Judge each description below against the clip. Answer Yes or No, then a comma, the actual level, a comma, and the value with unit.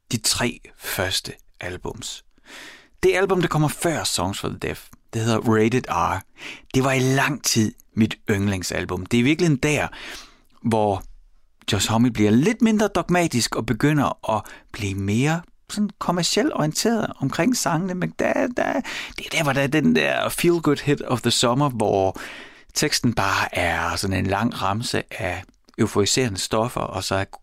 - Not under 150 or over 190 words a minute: Yes, average, 170 wpm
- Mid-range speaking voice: No, low, 130 Hz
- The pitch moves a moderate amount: No, wide, 8.6 semitones